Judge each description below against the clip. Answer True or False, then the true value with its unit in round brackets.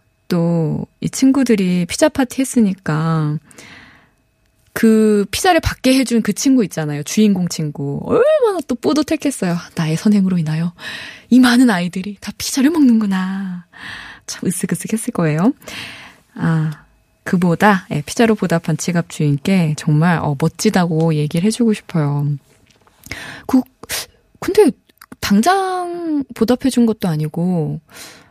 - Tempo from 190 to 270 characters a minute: True (260 characters per minute)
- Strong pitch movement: True (7.0 semitones)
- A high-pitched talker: True (195 Hz)